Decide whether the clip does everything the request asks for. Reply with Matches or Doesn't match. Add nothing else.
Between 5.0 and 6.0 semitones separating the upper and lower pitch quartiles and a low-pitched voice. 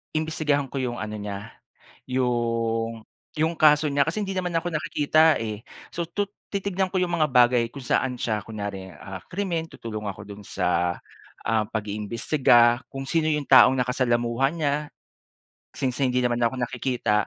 Matches